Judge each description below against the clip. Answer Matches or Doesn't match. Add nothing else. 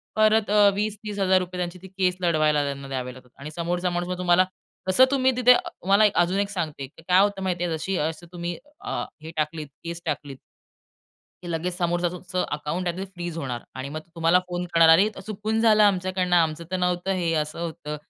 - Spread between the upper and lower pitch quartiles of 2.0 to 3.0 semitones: Matches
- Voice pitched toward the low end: Doesn't match